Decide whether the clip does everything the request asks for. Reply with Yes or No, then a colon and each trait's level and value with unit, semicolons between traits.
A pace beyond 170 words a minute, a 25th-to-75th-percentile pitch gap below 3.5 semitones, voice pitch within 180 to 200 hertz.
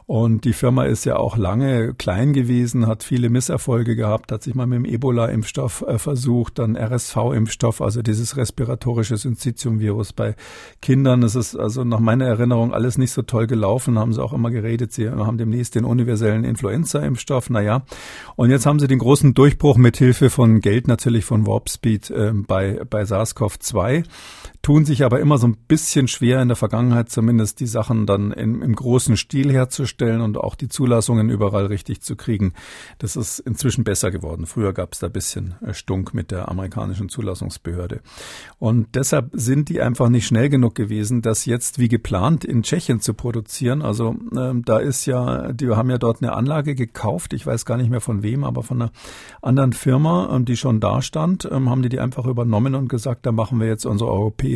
No: fast, 190 wpm; narrow, 2.6 semitones; low, 120 Hz